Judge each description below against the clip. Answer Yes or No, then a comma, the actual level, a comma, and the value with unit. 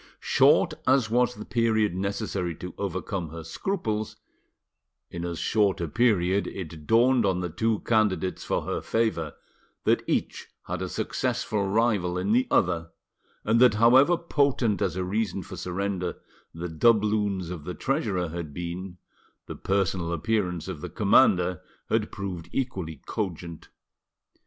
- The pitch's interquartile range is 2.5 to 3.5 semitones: No, average, 4.2 semitones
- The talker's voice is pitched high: No, very low, 95 Hz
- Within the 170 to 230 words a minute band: No, average, 145 wpm